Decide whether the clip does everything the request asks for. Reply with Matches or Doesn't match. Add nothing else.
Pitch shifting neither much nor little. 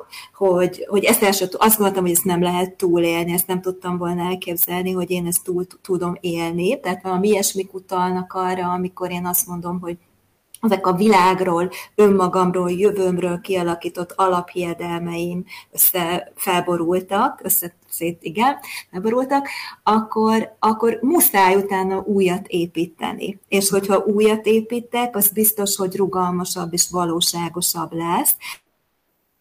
Doesn't match